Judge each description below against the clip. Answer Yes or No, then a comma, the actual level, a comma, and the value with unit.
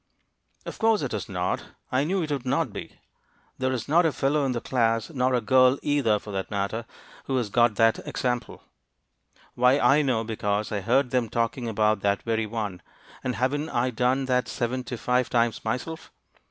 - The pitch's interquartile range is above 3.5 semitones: No, average, 3.0 semitones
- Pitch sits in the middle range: No, low, 125 Hz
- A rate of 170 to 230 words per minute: Yes, average, 190 wpm